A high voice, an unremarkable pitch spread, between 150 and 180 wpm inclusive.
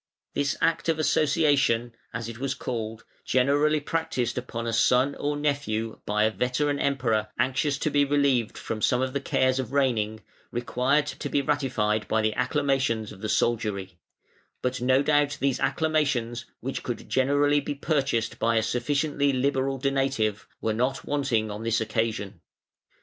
No: low, 130 Hz; average, 3.9 semitones; average, 160 wpm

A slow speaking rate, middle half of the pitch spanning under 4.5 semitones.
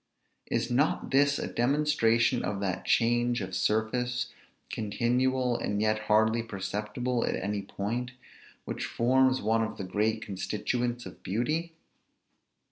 Yes: slow, 125 wpm; average, 2.8 semitones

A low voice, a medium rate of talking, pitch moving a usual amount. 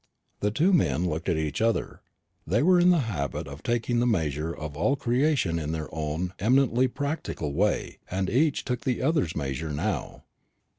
No: low, 105 Hz; average, 180 wpm; wide, 8.8 semitones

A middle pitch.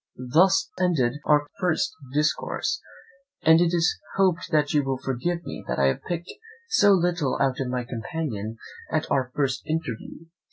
Yes: medium, 150 Hz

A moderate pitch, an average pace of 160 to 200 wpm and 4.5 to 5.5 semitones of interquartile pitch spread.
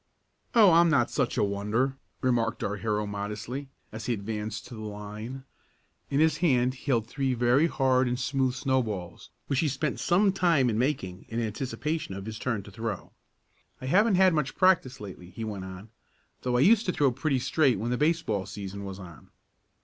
No: low, 125 Hz; average, 190 wpm; average, 5.0 semitones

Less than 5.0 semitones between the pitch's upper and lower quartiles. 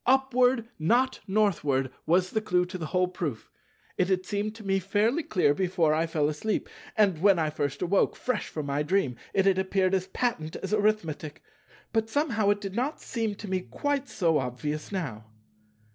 No: average, 5.3 semitones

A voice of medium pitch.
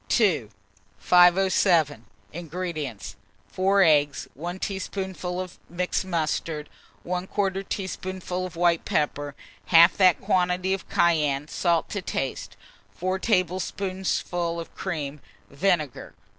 Yes: medium, 180 Hz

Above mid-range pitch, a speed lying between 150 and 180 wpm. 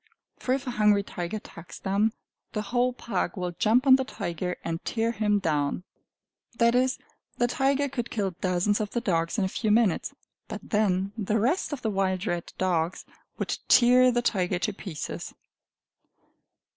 Yes: high, 210 Hz; average, 170 wpm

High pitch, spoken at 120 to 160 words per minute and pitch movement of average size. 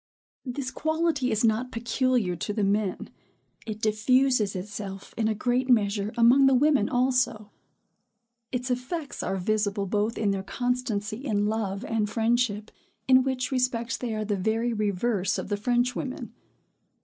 Yes: high, 225 Hz; average, 150 wpm; average, 3.4 semitones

